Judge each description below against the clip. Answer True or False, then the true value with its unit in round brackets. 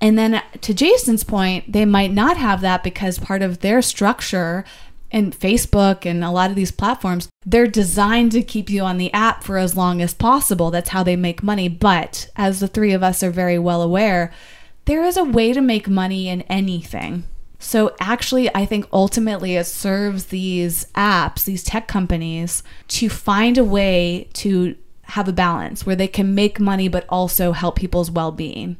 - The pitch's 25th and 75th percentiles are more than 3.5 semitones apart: False (3.0 semitones)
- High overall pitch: True (195 Hz)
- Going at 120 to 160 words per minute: False (190 wpm)